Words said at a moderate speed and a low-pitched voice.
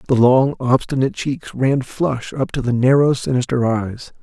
Yes: average, 170 wpm; low, 130 Hz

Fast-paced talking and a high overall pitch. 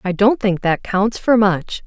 Yes: fast, 225 wpm; high, 200 Hz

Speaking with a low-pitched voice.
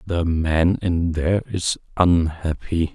Yes: very low, 85 Hz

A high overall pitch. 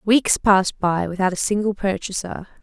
Yes: high, 195 Hz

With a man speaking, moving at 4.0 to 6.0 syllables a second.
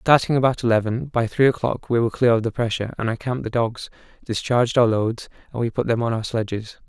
No: male; 6.3 syllables/s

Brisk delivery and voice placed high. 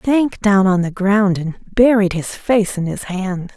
Yes: fast, 220 wpm; high, 195 Hz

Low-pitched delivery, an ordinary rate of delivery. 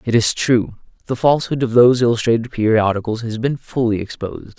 Yes: low, 115 Hz; average, 185 wpm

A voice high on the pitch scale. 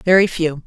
No: medium, 170 Hz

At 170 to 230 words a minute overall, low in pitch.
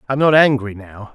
No: fast, 260 wpm; low, 125 Hz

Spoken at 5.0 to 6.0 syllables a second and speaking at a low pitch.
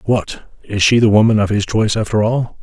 Yes: 5.5 syllables/s; low, 105 Hz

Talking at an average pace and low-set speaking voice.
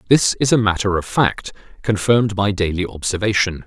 Yes: average, 165 wpm; low, 100 Hz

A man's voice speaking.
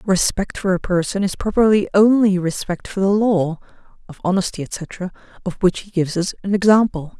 No: female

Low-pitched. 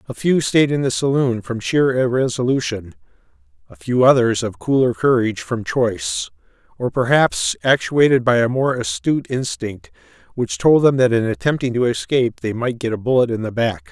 Yes: low, 125 Hz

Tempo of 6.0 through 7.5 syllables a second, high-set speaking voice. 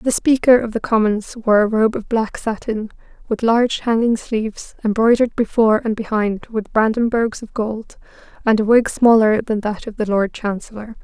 No: 5.0 syllables/s; high, 220 Hz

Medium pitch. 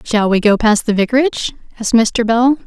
No: high, 230 Hz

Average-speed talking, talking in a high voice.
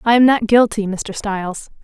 Yes: average, 195 wpm; high, 215 Hz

